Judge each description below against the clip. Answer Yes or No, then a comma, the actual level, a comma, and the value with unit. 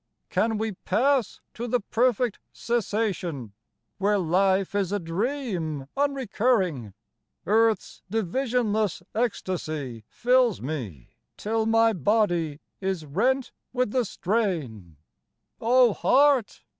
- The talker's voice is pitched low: No, high, 210 Hz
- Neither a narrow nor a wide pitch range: No, wide, 5.8 semitones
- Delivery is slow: Yes, slow, 100 wpm